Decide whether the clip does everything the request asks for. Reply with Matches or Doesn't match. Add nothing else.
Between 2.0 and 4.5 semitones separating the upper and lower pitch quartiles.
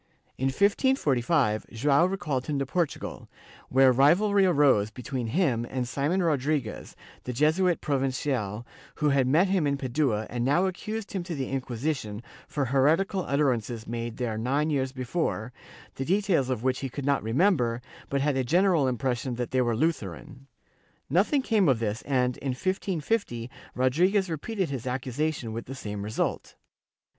Doesn't match